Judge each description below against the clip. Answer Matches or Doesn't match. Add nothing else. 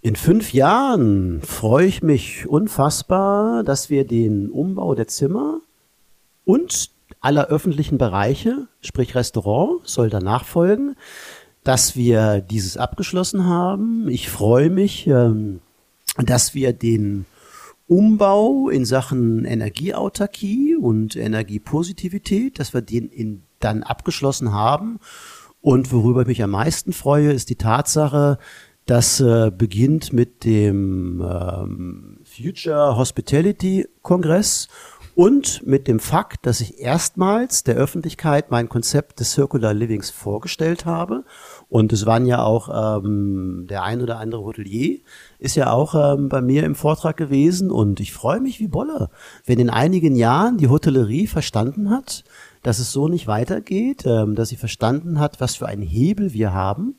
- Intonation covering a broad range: Matches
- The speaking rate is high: Doesn't match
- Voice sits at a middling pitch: Doesn't match